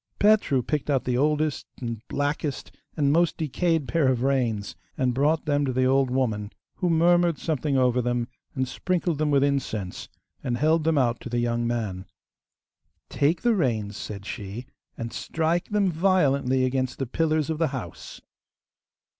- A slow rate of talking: No, average, 165 wpm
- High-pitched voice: No, low, 135 Hz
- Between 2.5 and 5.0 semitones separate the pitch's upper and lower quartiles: Yes, average, 4.5 semitones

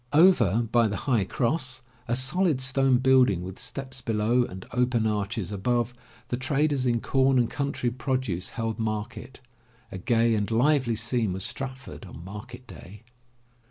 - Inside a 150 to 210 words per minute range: Yes, average, 155 wpm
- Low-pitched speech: Yes, low, 120 Hz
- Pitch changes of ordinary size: Yes, average, 3.5 semitones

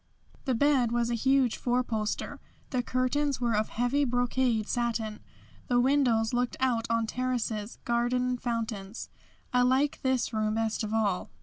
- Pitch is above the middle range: Yes, high, 240 Hz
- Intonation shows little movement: Yes, narrow, 2.3 semitones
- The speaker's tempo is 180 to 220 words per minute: No, average, 155 wpm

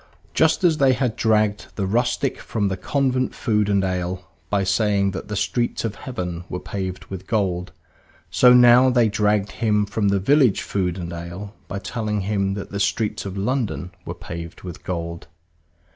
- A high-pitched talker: No, low, 100 Hz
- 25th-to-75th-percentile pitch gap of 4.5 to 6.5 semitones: No, average, 3.8 semitones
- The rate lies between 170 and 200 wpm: Yes, average, 175 wpm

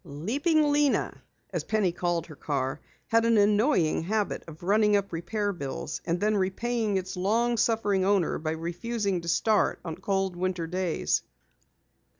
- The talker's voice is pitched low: No, high, 195 Hz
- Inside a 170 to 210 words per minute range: No, average, 155 wpm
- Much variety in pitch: No, average, 4.2 semitones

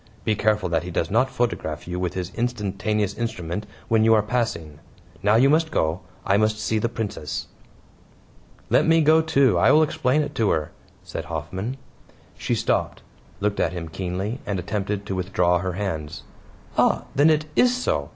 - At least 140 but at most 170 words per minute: No, average, 180 wpm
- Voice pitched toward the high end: No, low, 105 Hz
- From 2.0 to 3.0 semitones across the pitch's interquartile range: No, average, 5.2 semitones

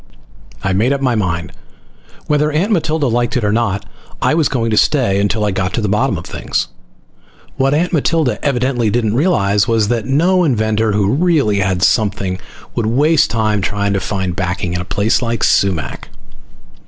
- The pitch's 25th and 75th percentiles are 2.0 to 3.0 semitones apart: No, wide, 5.5 semitones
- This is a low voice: Yes, low, 110 Hz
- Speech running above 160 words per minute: Yes, average, 180 wpm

